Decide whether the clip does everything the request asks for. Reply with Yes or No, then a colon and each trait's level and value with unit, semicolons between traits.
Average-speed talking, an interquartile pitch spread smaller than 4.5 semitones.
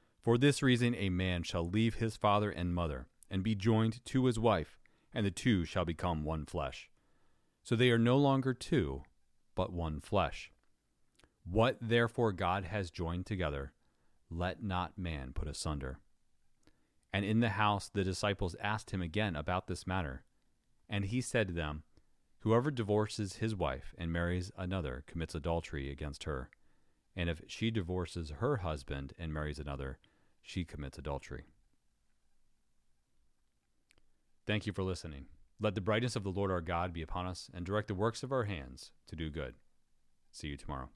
No: average, 165 wpm; average, 5.3 semitones